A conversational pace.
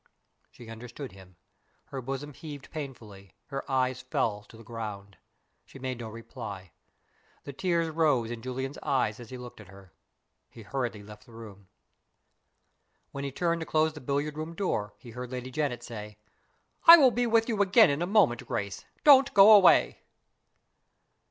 Yes: average, 170 wpm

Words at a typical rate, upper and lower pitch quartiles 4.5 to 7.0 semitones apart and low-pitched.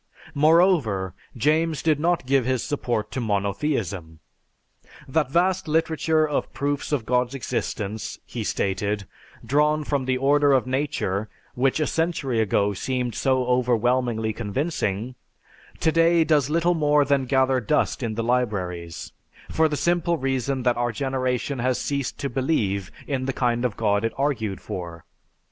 Yes: average, 145 wpm; average, 4.8 semitones; low, 130 Hz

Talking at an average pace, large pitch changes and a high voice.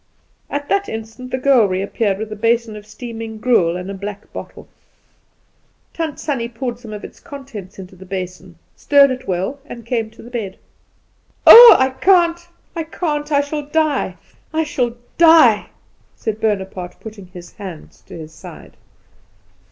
Yes: average, 160 wpm; wide, 6.2 semitones; high, 230 Hz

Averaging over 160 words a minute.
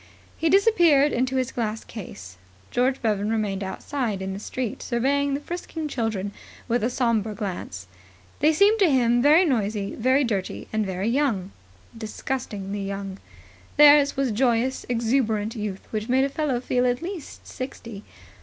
No: average, 155 wpm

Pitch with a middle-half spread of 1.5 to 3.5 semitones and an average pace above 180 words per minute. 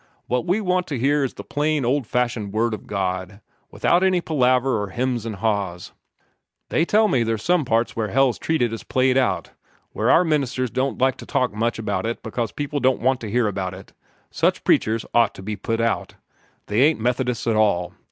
No: average, 4.0 semitones; fast, 205 wpm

